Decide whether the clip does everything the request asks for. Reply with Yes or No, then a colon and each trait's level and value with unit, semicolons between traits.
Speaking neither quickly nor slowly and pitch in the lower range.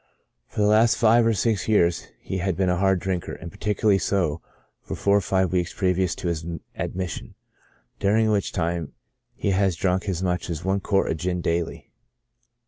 Yes: average, 185 wpm; very low, 95 Hz